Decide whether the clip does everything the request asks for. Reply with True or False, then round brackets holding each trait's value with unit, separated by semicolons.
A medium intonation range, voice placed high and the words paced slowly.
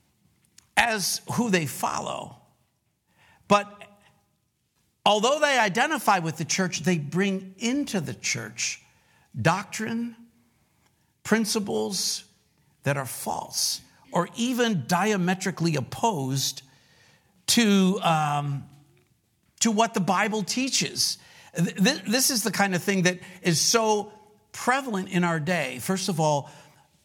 True (4.6 semitones; 195 Hz; 105 wpm)